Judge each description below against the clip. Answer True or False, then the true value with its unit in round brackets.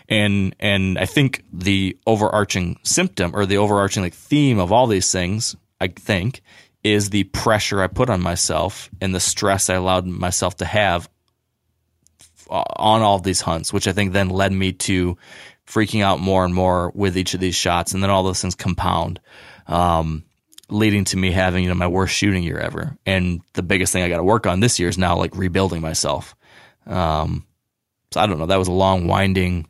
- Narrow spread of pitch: True (2.2 semitones)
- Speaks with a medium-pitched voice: False (95 Hz)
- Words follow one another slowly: False (200 wpm)